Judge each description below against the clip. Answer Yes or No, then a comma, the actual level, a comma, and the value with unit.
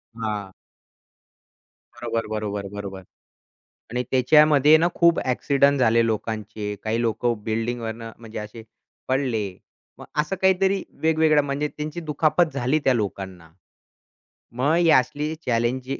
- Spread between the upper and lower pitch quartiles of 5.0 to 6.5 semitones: Yes, average, 5.3 semitones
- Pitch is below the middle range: Yes, low, 125 Hz